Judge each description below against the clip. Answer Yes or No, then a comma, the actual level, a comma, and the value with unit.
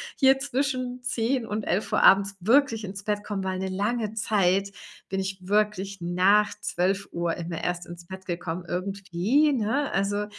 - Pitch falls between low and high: No, high, 200 Hz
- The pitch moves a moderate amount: Yes, average, 3.1 semitones